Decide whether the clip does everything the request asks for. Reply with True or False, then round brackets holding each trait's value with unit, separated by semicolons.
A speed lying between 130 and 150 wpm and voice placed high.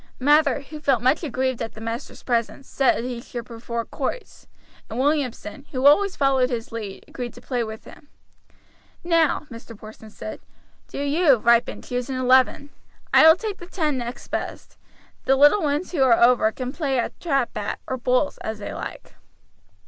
False (180 wpm; 255 Hz)